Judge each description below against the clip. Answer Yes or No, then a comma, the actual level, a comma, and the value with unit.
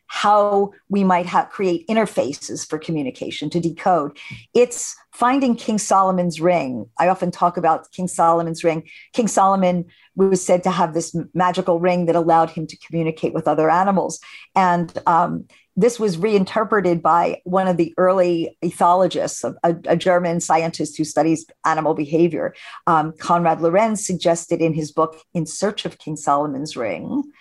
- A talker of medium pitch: Yes, medium, 175 Hz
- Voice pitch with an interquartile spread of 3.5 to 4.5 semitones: No, average, 2.9 semitones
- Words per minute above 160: No, average, 155 wpm